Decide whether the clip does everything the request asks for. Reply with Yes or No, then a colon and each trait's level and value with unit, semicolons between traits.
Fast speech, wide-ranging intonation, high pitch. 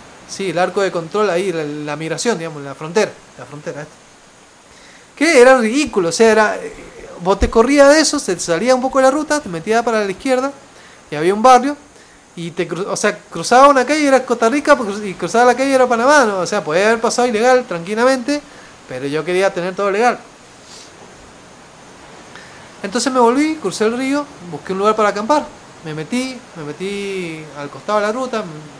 Yes: fast, 195 wpm; wide, 6.2 semitones; high, 215 Hz